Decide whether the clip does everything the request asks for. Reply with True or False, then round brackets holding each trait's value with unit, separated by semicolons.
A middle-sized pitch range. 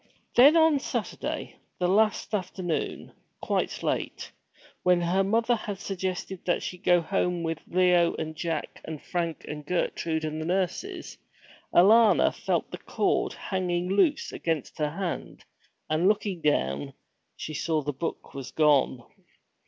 True (3.6 semitones)